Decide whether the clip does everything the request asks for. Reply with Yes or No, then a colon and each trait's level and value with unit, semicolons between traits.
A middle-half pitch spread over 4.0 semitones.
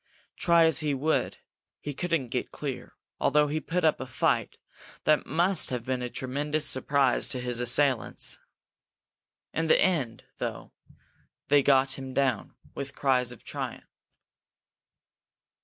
No: average, 3.2 semitones